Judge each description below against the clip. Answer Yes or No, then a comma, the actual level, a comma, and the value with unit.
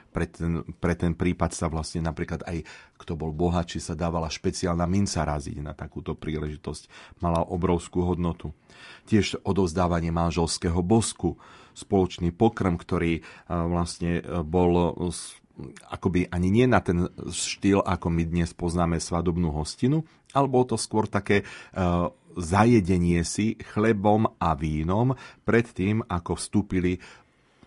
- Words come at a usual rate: Yes, average, 125 wpm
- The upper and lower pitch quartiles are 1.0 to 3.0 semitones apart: Yes, narrow, 2.5 semitones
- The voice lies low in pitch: Yes, very low, 90 Hz